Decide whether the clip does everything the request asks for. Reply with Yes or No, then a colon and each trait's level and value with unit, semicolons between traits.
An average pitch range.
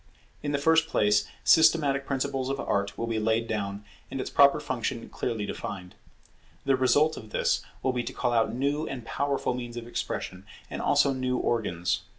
Yes: average, 3.9 semitones